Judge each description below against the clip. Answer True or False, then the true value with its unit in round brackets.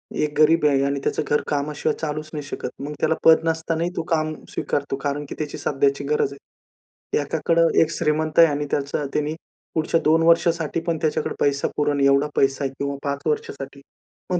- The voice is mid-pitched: True (150 Hz)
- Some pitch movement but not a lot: False (2.2 semitones)